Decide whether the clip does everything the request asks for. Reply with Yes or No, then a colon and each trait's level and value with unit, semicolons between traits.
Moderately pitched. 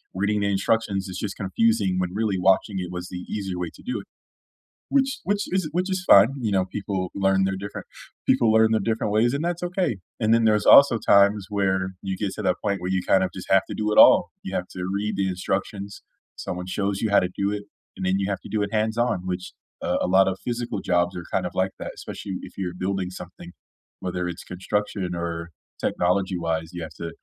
No: very low, 95 Hz